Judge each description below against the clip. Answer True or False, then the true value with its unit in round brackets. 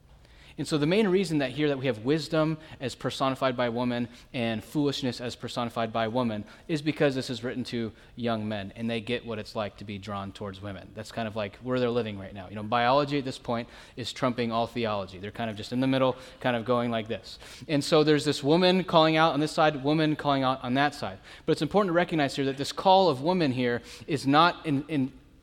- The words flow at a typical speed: False (245 wpm)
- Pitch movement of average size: True (4.3 semitones)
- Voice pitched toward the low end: True (125 Hz)